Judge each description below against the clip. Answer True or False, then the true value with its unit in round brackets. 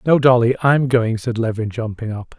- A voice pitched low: True (120 Hz)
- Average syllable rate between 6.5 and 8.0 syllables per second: False (5.0 syllables/s)